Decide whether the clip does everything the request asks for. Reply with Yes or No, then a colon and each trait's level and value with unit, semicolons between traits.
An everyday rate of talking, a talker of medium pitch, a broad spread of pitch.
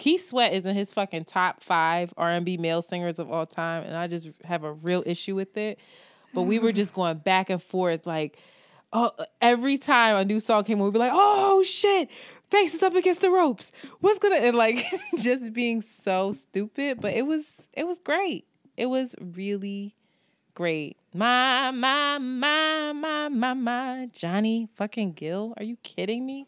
No: average, 190 wpm; high, 220 Hz; wide, 6.5 semitones